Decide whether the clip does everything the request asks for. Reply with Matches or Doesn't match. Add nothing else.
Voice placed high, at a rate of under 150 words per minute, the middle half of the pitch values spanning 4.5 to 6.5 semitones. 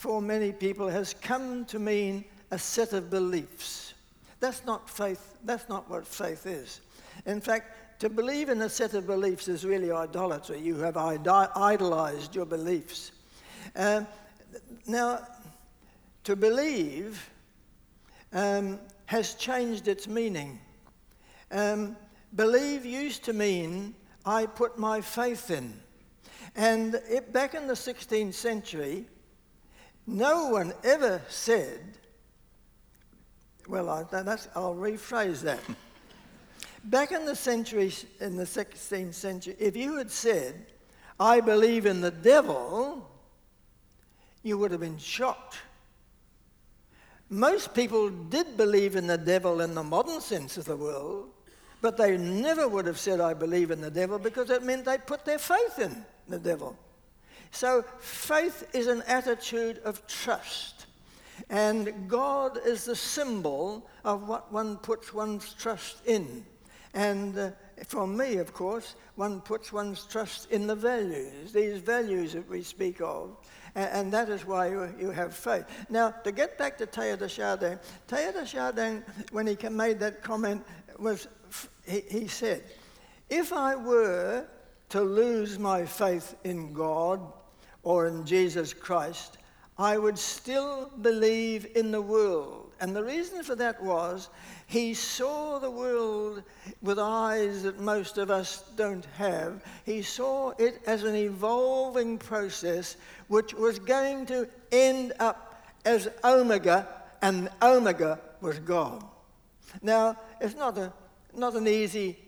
Doesn't match